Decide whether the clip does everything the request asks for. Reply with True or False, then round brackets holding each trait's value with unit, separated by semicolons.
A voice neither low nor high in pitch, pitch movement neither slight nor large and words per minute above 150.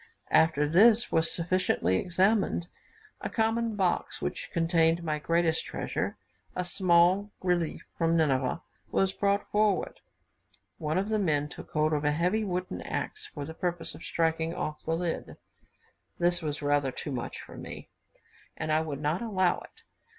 True (170 Hz; 3.3 semitones; 160 wpm)